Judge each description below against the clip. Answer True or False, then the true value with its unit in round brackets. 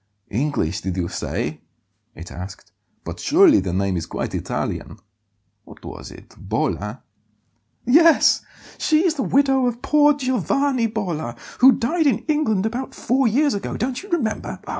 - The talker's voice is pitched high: True (245 Hz)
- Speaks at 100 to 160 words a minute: True (150 wpm)